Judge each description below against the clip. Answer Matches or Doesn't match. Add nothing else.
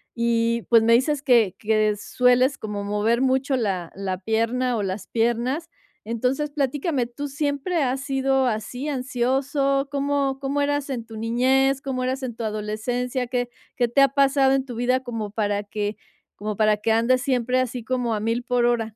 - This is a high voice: Matches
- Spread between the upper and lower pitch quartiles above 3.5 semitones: Doesn't match